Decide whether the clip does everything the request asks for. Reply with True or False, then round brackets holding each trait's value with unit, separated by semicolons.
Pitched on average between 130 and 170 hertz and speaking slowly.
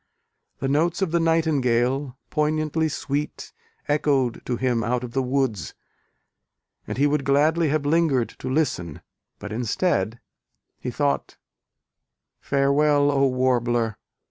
True (140 Hz; 120 wpm)